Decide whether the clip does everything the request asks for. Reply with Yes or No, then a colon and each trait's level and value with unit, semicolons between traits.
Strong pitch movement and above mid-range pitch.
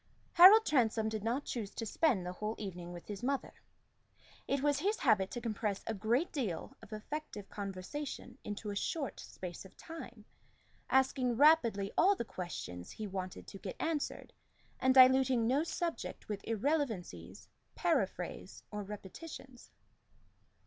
Yes: wide, 5.9 semitones; high, 230 Hz